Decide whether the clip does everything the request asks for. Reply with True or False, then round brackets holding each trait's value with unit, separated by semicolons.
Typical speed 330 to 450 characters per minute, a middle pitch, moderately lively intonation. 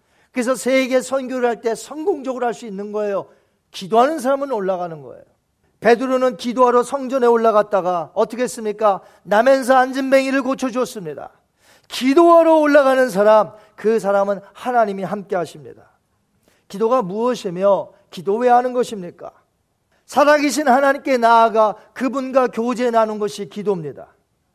False (340 characters per minute; 235 Hz; 4.0 semitones)